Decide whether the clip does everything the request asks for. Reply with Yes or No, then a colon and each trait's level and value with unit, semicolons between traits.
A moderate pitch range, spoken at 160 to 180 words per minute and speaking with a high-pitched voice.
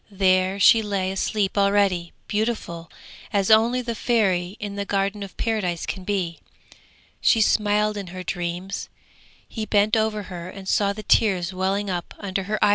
No: narrow, 2.3 semitones; average, 165 wpm; high, 200 Hz